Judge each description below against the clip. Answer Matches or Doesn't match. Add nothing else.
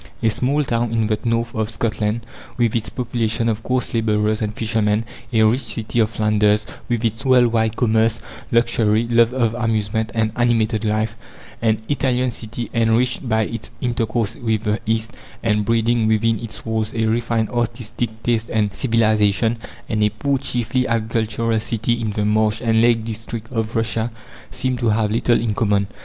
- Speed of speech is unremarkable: Matches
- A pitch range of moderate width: Doesn't match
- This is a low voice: Matches